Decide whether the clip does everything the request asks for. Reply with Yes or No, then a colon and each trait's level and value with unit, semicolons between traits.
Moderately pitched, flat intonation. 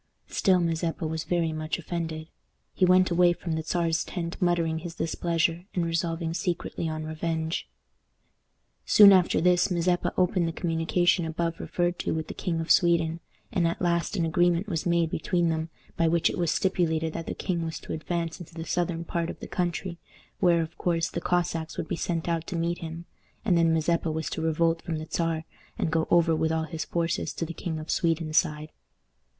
Yes: medium, 165 Hz; narrow, 1.3 semitones